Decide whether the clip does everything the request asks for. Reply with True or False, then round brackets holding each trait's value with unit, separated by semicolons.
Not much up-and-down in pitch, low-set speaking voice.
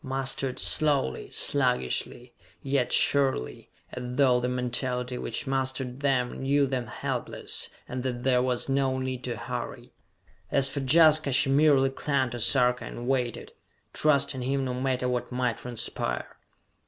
True (1.6 semitones; 130 Hz)